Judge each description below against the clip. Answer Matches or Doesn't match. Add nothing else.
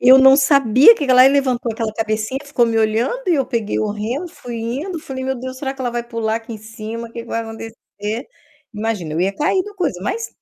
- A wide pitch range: Doesn't match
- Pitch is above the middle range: Matches